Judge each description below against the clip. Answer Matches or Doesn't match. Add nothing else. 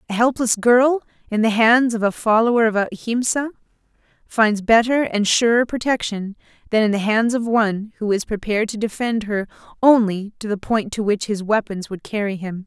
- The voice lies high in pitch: Matches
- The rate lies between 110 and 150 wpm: Doesn't match